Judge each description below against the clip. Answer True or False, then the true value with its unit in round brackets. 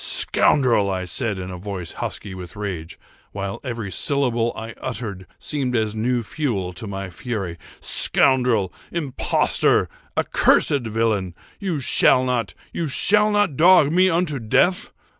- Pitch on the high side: False (115 Hz)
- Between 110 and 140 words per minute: True (135 wpm)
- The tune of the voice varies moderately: False (6.2 semitones)